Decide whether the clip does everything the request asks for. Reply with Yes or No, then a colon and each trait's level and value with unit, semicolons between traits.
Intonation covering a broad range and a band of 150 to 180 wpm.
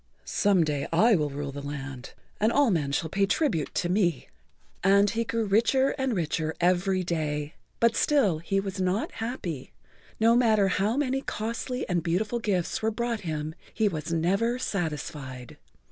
Yes: wide, 6.1 semitones; average, 165 wpm